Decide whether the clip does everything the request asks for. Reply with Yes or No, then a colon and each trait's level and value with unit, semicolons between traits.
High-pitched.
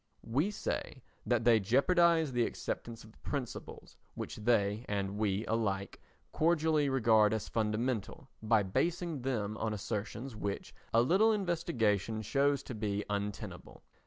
No: low, 115 Hz